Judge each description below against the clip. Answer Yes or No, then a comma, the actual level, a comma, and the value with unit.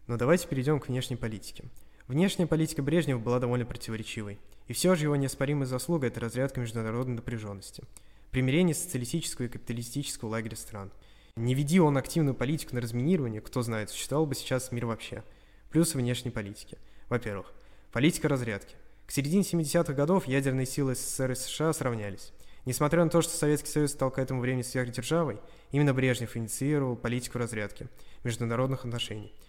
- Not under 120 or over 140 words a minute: No, average, 155 wpm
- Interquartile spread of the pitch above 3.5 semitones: Yes, average, 4.2 semitones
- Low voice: Yes, low, 125 Hz